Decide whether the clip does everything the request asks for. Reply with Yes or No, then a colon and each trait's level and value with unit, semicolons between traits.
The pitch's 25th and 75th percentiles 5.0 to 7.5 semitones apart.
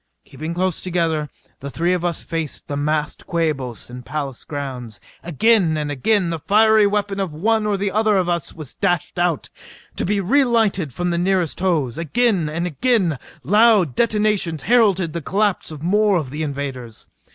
Yes: average, 5.3 semitones